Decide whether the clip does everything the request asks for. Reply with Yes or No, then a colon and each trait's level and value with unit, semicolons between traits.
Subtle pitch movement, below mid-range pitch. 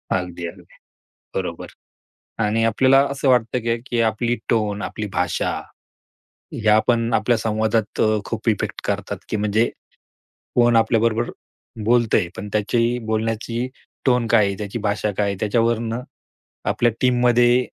Yes: narrow, 2.1 semitones; low, 115 Hz